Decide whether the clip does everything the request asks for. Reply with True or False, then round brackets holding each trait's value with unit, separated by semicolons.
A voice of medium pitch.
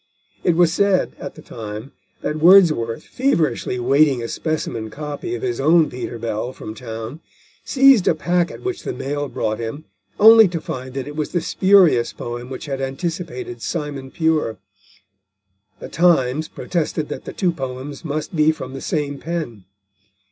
True (150 Hz)